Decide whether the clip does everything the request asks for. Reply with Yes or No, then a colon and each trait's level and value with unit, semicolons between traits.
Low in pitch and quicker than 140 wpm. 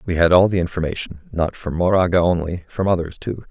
Yes: very low, 90 Hz; fast, 205 wpm